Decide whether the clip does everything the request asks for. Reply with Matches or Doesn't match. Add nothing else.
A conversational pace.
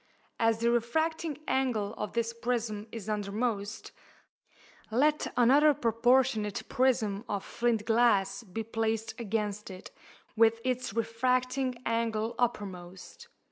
Doesn't match